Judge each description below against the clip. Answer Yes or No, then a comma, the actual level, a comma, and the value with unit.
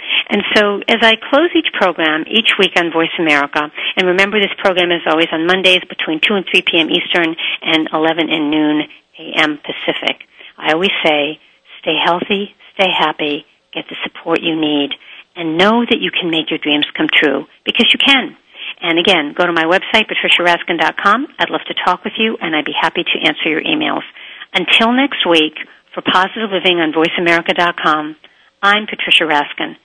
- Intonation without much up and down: No, average, 4.0 semitones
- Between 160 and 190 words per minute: Yes, average, 180 wpm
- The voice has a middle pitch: Yes, medium, 175 Hz